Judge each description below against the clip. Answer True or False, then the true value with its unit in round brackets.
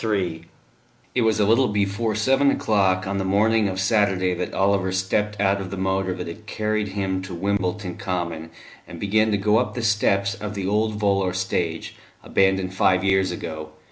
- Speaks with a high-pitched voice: False (100 Hz)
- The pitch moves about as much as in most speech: False (2.1 semitones)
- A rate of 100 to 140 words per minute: False (185 wpm)